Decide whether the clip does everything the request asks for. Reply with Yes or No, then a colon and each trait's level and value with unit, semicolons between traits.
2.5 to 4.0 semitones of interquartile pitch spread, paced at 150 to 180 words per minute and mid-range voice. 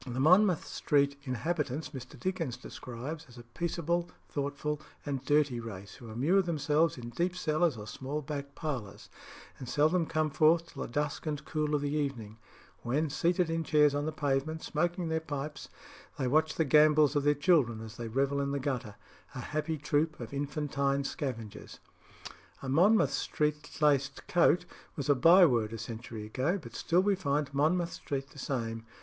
Yes: average, 3.3 semitones; average, 175 wpm; medium, 145 Hz